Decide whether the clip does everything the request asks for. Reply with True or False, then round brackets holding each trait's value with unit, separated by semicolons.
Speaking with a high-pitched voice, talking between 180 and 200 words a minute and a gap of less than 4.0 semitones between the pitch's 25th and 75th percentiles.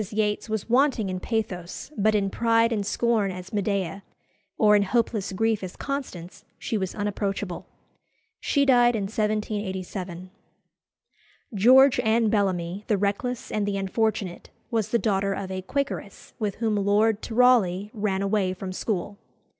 False (210 Hz; 145 wpm; 2.7 semitones)